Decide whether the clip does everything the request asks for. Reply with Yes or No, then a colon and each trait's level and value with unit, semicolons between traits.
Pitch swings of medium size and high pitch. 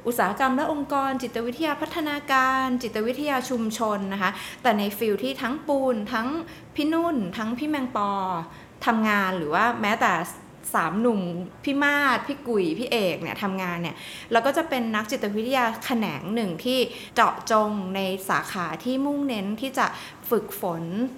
Yes: average, 4.5 semitones; high, 235 Hz